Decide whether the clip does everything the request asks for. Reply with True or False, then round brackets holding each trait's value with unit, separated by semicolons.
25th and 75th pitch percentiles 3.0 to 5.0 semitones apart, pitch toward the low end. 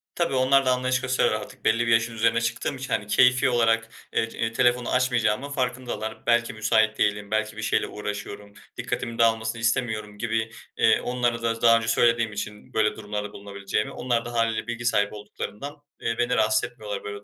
False (2.4 semitones; 115 Hz)